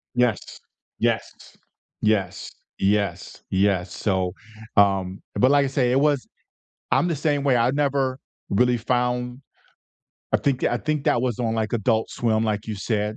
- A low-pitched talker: Yes, low, 120 Hz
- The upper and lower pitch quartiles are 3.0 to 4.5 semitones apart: Yes, average, 4.0 semitones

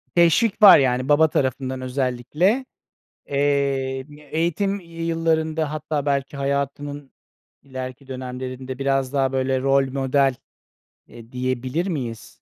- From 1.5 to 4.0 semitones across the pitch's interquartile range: Yes, average, 3.1 semitones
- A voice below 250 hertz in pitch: Yes, medium, 140 Hz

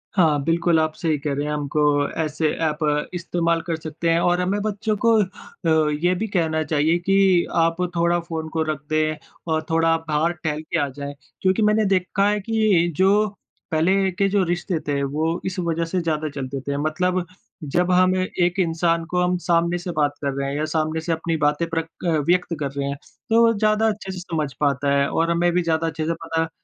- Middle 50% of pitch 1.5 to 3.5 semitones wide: Yes, average, 2.7 semitones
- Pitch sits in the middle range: Yes, medium, 165 Hz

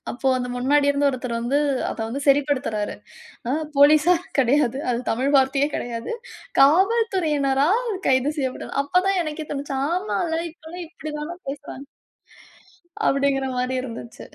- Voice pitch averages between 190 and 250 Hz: No, very high, 280 Hz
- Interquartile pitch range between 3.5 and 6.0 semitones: No, average, 3.0 semitones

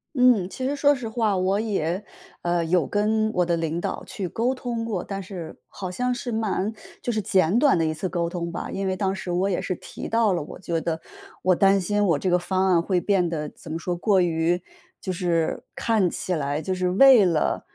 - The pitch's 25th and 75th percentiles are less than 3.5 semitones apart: No, average, 3.8 semitones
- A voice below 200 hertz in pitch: Yes, medium, 185 Hz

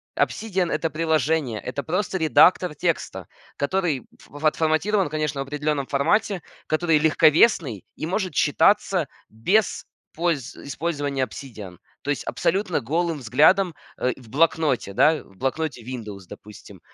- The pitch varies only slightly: No, average, 4.1 semitones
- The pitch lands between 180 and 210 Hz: No, medium, 155 Hz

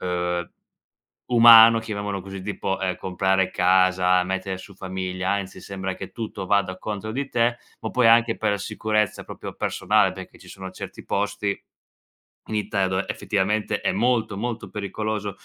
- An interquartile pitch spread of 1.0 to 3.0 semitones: Yes, narrow, 2.6 semitones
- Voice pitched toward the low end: Yes, low, 100 Hz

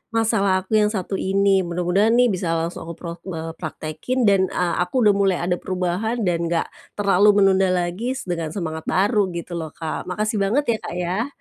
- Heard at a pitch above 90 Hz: Yes, medium, 185 Hz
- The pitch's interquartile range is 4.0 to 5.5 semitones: No, average, 3.2 semitones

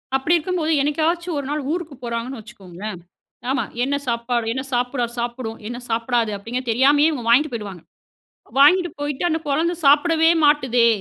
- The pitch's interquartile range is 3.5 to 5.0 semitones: Yes, average, 4.5 semitones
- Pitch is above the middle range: Yes, very high, 260 Hz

